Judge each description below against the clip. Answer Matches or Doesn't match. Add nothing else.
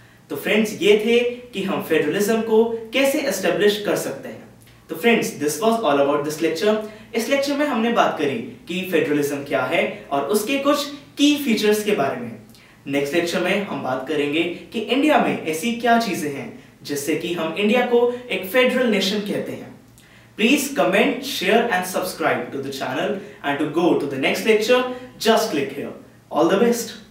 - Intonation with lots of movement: Matches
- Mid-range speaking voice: Doesn't match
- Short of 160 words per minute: Doesn't match